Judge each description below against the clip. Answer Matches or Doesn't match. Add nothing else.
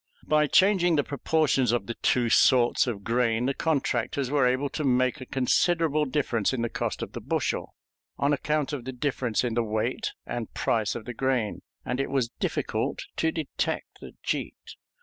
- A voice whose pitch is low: Matches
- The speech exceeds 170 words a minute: Matches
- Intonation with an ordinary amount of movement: Matches